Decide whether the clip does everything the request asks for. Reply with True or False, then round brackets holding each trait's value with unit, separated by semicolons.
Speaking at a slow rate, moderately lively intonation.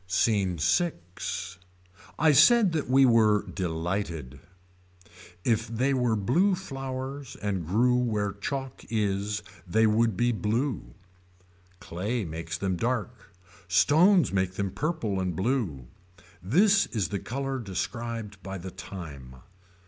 False (120 wpm; 5.7 semitones)